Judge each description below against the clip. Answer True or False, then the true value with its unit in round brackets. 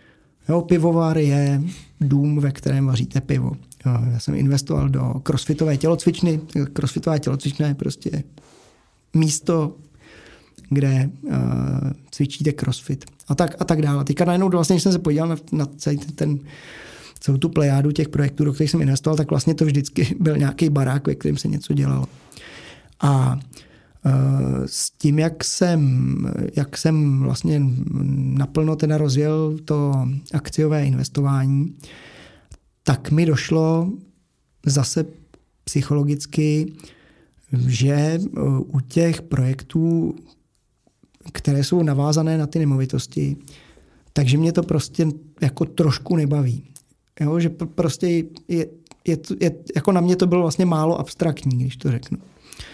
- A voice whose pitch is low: False (145 Hz)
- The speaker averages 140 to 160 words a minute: False (130 wpm)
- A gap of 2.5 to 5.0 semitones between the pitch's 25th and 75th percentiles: True (2.8 semitones)